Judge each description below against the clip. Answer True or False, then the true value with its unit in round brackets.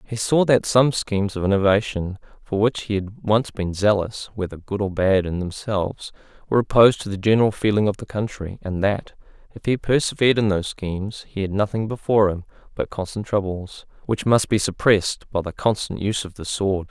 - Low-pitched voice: True (105 Hz)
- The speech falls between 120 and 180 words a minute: False (200 wpm)